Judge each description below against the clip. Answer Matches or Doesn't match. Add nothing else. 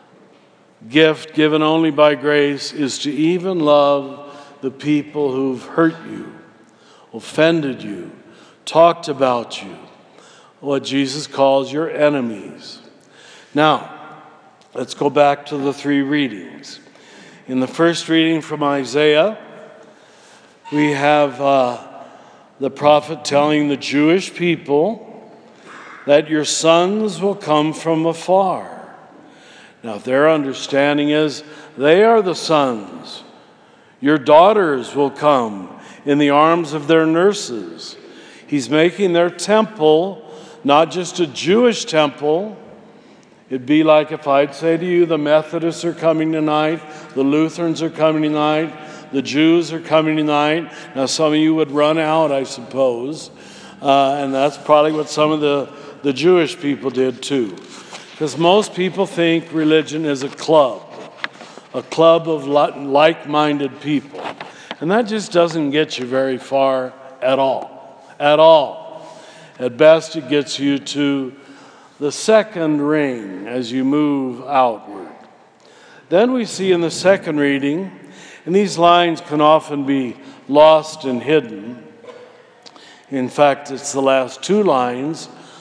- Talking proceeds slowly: Matches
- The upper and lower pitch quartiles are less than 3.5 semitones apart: Matches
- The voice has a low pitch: Doesn't match